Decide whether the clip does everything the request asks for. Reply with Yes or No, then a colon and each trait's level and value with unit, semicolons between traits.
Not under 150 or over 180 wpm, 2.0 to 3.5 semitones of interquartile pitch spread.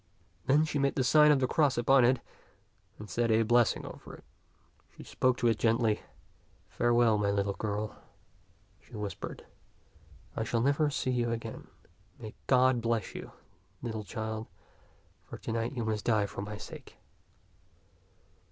Yes: average, 160 wpm; average, 2.9 semitones